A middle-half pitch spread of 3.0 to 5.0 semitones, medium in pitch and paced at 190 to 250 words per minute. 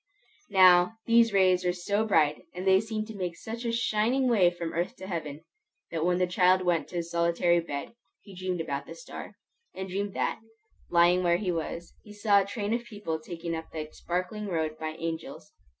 Yes: average, 3.4 semitones; medium, 180 Hz; average, 200 wpm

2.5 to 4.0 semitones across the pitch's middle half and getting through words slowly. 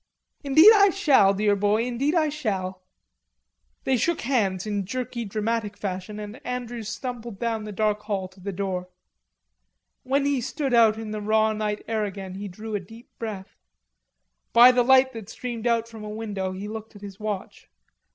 No: average, 3.1 semitones; average, 180 wpm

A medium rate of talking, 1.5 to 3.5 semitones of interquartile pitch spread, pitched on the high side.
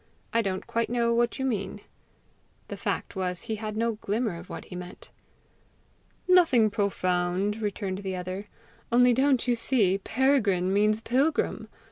No: average, 150 wpm; average, 3.9 semitones; high, 215 Hz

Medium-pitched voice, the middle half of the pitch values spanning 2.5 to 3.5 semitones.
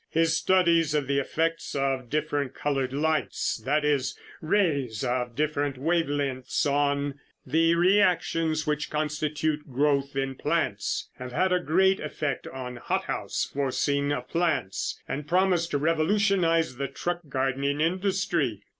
Yes: medium, 150 Hz; average, 3.2 semitones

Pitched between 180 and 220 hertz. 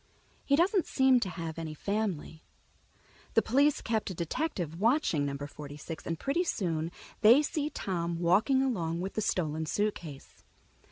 Yes: medium, 185 Hz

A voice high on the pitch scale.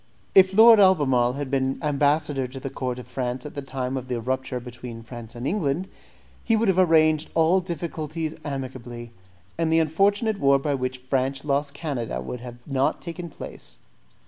No: medium, 140 Hz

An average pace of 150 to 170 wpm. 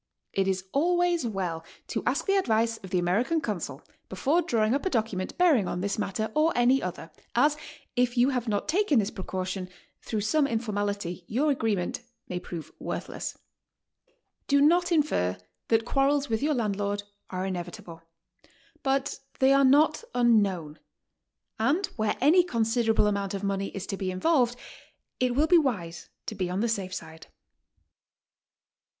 Yes: average, 160 wpm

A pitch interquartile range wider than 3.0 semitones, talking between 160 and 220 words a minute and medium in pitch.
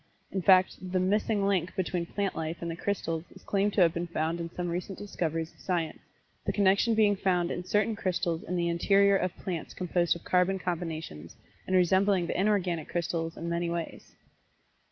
No: narrow, 2.4 semitones; average, 190 wpm; medium, 180 Hz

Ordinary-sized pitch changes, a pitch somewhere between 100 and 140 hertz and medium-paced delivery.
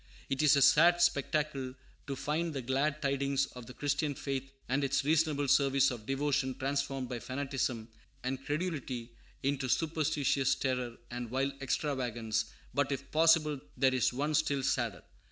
No: narrow, 2.2 semitones; low, 135 Hz; average, 155 wpm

